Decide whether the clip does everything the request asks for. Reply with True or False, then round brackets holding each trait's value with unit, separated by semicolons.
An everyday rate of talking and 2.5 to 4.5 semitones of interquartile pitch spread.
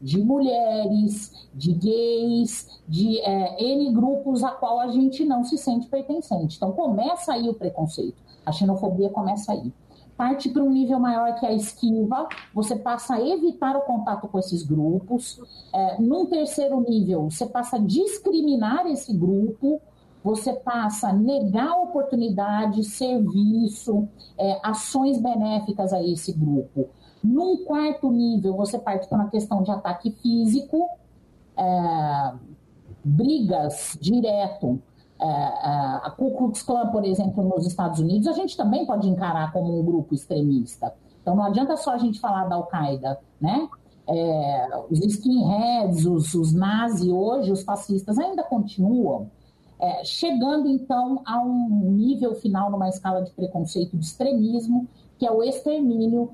False (145 wpm; 5.1 semitones)